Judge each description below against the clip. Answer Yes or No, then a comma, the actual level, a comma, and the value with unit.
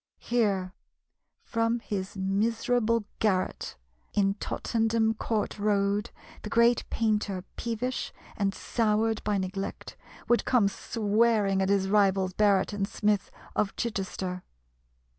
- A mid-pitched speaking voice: No, high, 210 Hz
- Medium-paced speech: No, slow, 110 wpm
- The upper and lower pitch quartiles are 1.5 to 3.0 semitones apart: Yes, narrow, 2.6 semitones